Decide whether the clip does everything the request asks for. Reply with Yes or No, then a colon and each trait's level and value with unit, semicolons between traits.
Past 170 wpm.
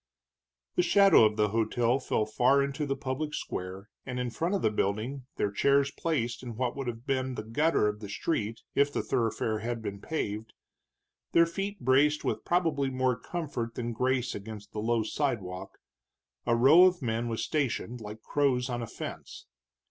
Yes: average, 180 wpm